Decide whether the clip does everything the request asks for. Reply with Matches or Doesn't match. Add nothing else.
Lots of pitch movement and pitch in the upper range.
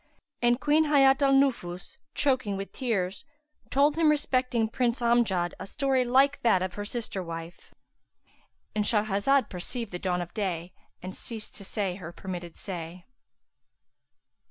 Matches